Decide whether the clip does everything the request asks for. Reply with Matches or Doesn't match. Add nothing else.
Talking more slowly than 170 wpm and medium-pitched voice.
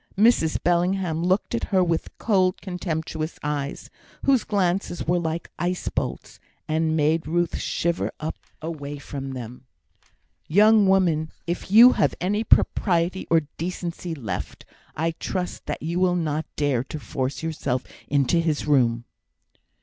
Matches